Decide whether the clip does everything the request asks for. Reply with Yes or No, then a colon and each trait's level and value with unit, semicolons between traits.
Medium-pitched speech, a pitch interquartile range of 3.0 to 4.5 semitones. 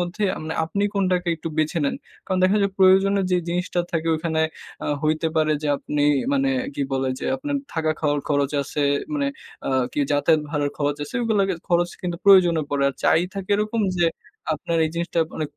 Yes: medium, 170 Hz; average, 3.8 semitones